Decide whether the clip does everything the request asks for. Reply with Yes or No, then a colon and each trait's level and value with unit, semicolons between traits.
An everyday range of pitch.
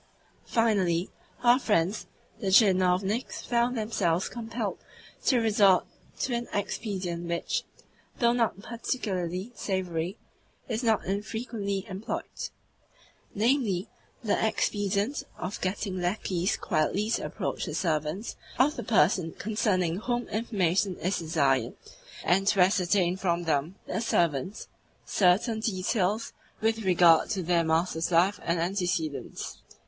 Yes: average, 4.0 semitones